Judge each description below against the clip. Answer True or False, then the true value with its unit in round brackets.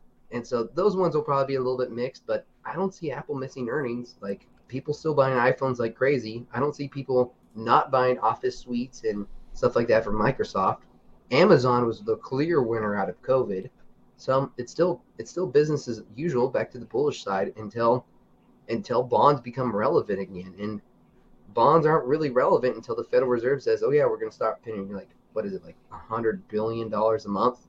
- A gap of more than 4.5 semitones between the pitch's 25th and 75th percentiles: True (5.0 semitones)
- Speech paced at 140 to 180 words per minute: False (205 wpm)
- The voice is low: True (125 Hz)